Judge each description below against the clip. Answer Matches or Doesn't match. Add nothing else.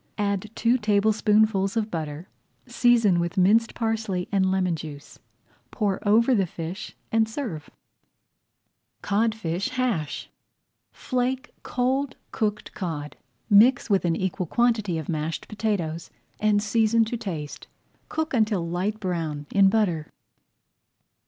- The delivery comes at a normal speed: Doesn't match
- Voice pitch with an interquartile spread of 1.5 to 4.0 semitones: Doesn't match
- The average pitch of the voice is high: Matches